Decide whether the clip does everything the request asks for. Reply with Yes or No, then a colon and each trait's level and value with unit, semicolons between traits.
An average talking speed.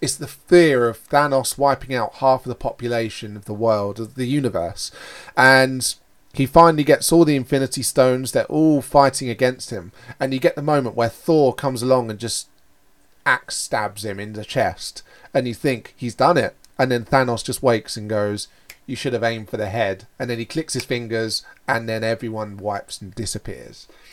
Yes: average, 195 wpm